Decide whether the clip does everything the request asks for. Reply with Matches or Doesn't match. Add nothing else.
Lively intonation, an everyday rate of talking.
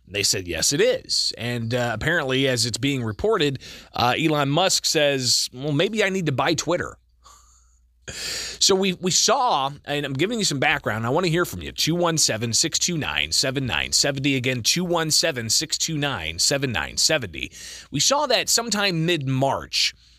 Matches